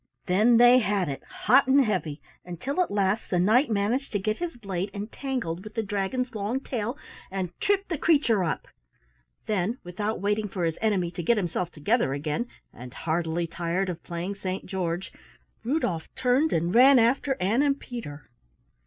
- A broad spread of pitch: Yes, wide, 5.9 semitones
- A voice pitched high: Yes, high, 205 Hz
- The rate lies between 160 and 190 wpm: Yes, average, 170 wpm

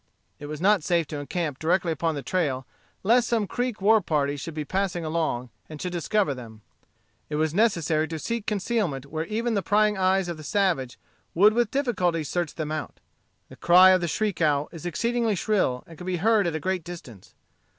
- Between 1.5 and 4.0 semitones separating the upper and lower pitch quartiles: No, average, 5.1 semitones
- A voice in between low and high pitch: Yes, medium, 175 Hz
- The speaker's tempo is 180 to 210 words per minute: Yes, average, 200 wpm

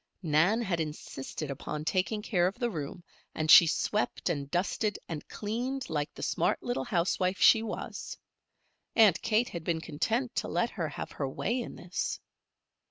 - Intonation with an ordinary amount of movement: No, wide, 6.1 semitones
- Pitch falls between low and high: Yes, medium, 180 Hz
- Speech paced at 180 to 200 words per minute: No, average, 165 wpm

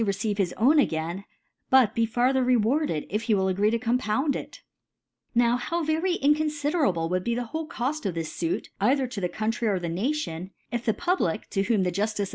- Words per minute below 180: No, fast, 205 wpm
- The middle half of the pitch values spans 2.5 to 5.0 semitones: No, wide, 5.6 semitones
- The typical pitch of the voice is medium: No, high, 230 Hz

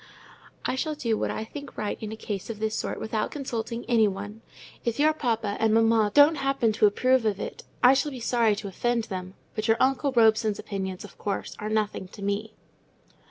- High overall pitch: Yes, high, 220 Hz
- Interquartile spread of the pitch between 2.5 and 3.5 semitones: Yes, average, 2.9 semitones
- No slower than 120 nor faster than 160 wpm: No, fast, 205 wpm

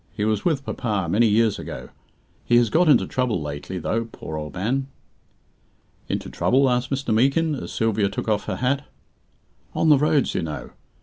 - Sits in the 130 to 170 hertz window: No, low, 115 Hz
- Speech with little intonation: No, average, 5.1 semitones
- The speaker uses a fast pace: No, average, 180 wpm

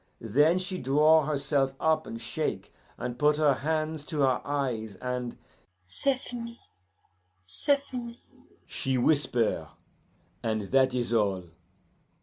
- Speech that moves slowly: Yes, slow, 125 wpm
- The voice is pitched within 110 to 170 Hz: Yes, medium, 140 Hz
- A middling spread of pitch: Yes, average, 4.6 semitones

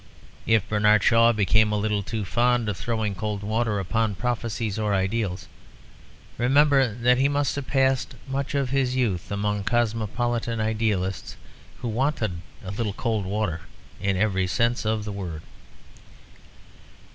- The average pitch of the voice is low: Yes, low, 110 Hz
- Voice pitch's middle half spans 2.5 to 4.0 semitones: Yes, average, 2.9 semitones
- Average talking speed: Yes, average, 145 wpm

